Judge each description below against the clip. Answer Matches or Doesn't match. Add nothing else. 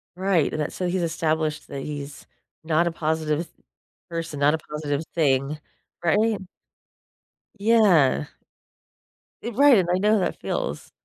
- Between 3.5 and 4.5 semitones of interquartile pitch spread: Matches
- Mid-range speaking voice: Matches